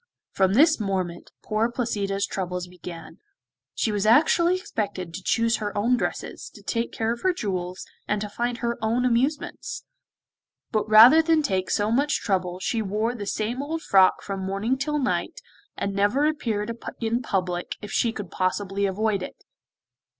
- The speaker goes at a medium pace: Yes, average, 165 wpm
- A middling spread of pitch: Yes, average, 3.8 semitones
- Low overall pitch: No, high, 215 Hz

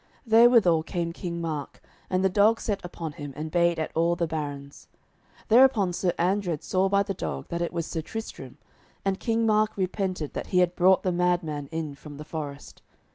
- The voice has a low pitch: No, medium, 175 Hz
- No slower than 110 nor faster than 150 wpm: No, average, 195 wpm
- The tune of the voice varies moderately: Yes, average, 3.7 semitones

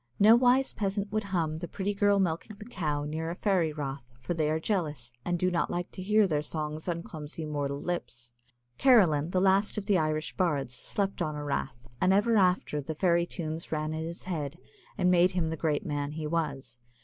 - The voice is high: No, medium, 165 Hz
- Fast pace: Yes, fast, 210 wpm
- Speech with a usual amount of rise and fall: Yes, average, 4.1 semitones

